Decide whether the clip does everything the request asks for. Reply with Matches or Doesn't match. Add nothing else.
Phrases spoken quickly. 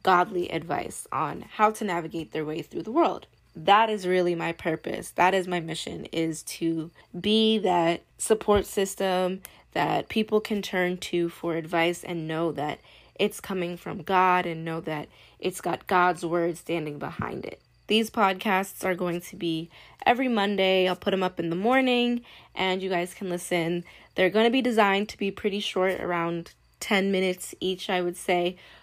Doesn't match